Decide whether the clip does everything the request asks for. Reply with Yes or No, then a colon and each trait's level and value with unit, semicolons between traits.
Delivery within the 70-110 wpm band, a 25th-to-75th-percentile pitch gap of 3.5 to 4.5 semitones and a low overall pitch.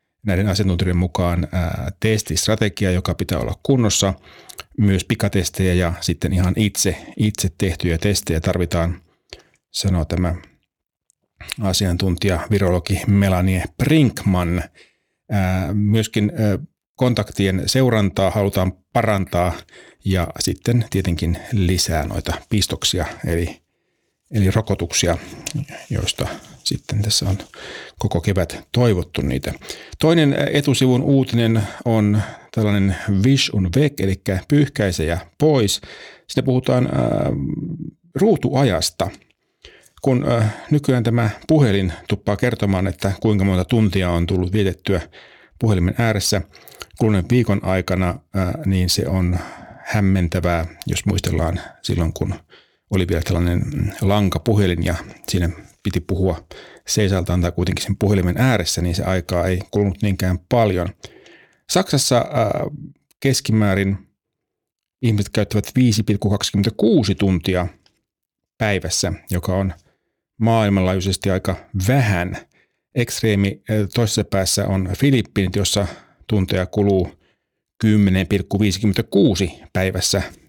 No: average, 100 wpm; average, 3.1 semitones; low, 100 Hz